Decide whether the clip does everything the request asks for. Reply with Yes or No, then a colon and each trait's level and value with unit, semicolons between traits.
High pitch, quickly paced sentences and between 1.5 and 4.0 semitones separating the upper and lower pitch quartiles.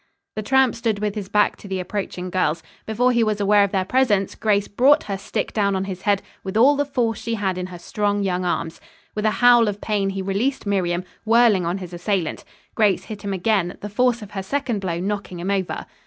Yes: high, 205 Hz; fast, 230 wpm; average, 2.8 semitones